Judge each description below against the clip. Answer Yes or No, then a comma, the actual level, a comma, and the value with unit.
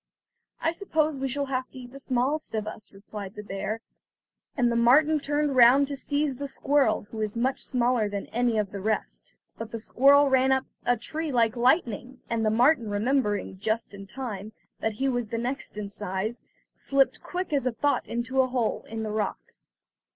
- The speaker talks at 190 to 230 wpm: Yes, average, 195 wpm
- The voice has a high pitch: Yes, high, 245 Hz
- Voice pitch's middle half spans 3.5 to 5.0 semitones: Yes, average, 4.0 semitones